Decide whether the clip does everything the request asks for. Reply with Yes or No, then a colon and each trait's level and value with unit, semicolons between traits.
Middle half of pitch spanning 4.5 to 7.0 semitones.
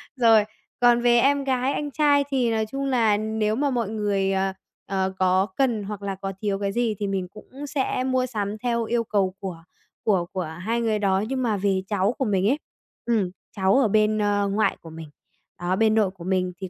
No: average, 3.7 semitones